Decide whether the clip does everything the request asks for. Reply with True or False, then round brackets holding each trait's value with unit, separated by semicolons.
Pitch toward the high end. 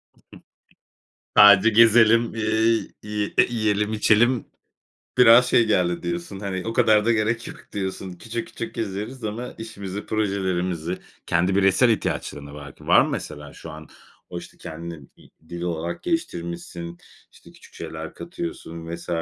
False (100 Hz)